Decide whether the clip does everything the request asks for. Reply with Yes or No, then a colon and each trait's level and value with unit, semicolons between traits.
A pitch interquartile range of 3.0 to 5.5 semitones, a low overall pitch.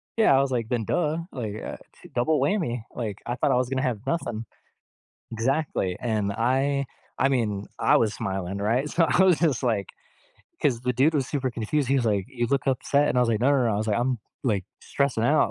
Yes: average, 3.8 semitones; low, 125 Hz